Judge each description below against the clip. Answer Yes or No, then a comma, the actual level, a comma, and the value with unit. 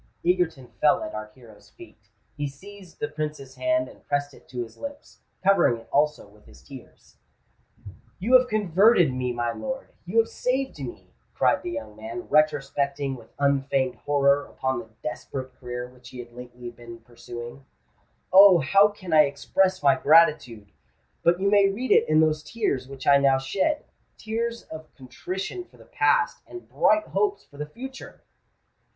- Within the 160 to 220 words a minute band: Yes, average, 165 wpm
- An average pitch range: No, wide, 7.6 semitones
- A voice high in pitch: No, medium, 145 Hz